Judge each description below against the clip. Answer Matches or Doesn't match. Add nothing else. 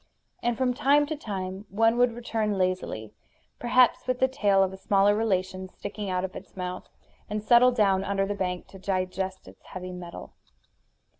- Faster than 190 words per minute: Doesn't match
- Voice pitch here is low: Doesn't match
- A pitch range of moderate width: Matches